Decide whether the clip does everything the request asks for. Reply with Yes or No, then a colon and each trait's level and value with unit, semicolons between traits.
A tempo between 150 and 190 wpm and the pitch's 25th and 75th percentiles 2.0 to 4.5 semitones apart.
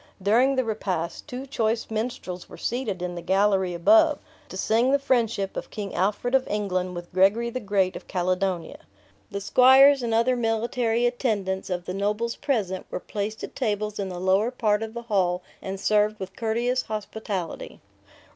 Yes: average, 175 wpm; average, 3.9 semitones